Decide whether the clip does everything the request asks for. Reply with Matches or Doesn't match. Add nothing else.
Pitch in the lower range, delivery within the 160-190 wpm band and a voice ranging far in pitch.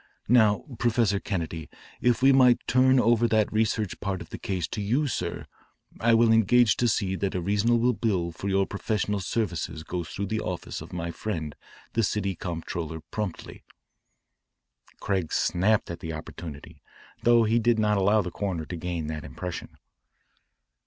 Doesn't match